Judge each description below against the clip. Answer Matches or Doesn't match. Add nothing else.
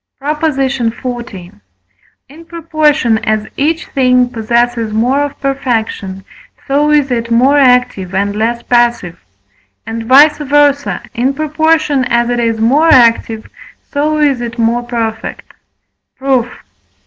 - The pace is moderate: Doesn't match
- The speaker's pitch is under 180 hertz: Doesn't match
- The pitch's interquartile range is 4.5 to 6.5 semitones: Doesn't match